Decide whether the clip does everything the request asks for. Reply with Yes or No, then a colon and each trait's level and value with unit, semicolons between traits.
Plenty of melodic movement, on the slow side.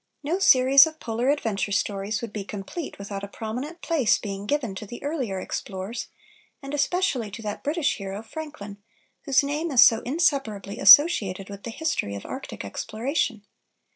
No: wide, 6.3 semitones; average, 165 wpm